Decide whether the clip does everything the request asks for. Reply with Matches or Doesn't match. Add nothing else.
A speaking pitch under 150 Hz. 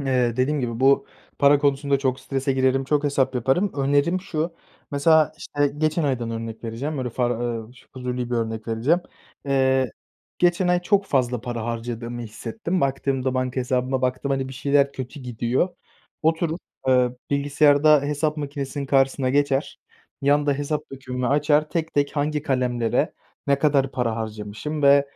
Matches